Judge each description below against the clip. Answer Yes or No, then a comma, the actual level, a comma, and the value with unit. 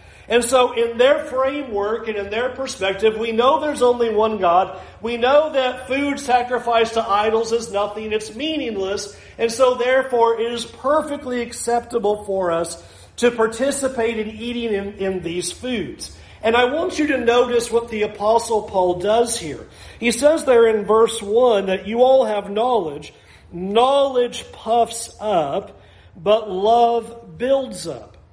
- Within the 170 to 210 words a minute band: No, average, 155 wpm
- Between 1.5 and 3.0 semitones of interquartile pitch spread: Yes, average, 2.7 semitones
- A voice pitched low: No, high, 230 Hz